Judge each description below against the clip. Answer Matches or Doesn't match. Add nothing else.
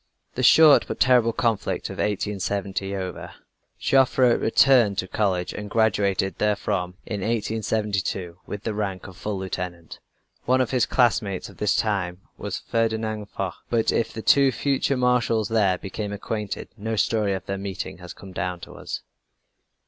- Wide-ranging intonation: Doesn't match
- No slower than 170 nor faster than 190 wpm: Doesn't match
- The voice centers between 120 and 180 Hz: Doesn't match